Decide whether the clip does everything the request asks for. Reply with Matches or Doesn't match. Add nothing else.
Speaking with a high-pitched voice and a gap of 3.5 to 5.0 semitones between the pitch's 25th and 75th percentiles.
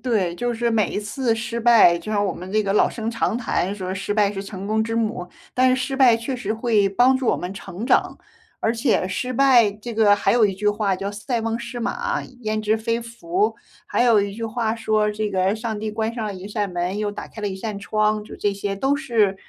Doesn't match